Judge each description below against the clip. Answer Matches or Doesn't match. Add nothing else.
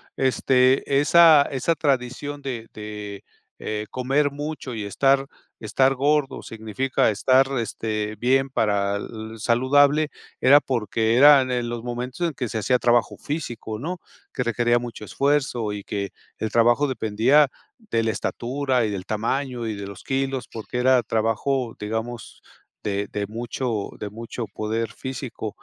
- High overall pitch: Doesn't match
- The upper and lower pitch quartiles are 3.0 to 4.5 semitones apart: Matches